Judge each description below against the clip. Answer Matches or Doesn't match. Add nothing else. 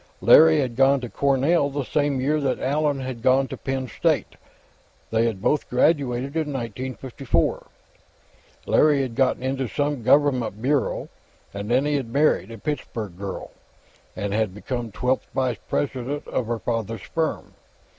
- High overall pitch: Doesn't match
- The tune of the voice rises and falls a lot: Doesn't match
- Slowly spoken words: Doesn't match